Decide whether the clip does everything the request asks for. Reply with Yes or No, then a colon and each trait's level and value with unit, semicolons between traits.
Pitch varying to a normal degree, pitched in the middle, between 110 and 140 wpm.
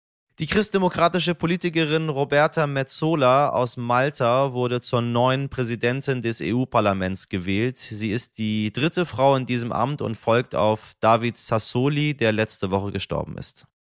No: average, 4.6 semitones; low, 125 Hz; average, 135 wpm